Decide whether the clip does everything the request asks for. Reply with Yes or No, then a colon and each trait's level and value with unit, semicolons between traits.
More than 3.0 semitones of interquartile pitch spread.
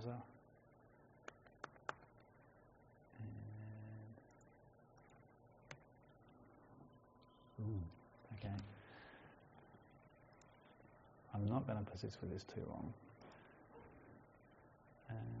No: narrow, 2.5 semitones